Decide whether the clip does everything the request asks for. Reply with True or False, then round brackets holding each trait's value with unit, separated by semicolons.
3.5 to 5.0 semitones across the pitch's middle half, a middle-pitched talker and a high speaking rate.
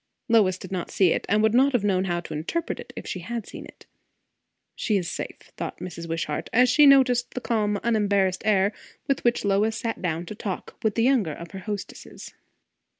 False (4.2 semitones; 205 Hz; 210 wpm)